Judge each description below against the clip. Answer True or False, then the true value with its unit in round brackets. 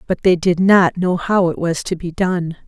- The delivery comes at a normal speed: False (245 wpm)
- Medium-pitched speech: True (175 Hz)